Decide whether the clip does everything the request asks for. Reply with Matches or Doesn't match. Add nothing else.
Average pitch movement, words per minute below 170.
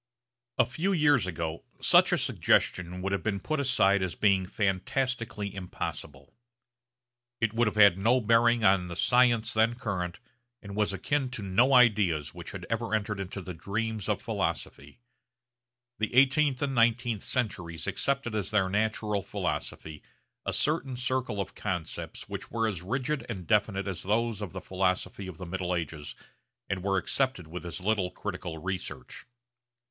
Matches